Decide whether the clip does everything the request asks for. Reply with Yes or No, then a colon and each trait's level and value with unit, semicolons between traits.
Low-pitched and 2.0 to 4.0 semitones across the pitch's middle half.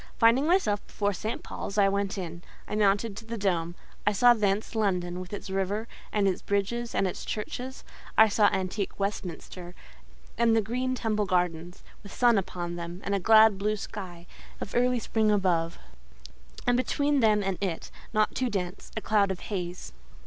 No: high, 205 Hz; average, 3.2 semitones